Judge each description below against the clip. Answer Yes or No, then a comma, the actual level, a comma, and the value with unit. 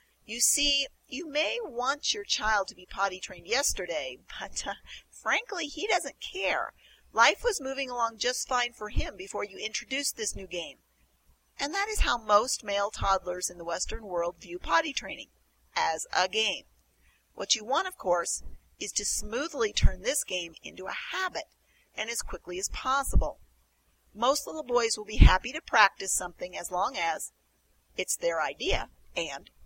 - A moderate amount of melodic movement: No, wide, 8.1 semitones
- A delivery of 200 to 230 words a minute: No, average, 170 wpm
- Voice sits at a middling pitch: No, high, 235 Hz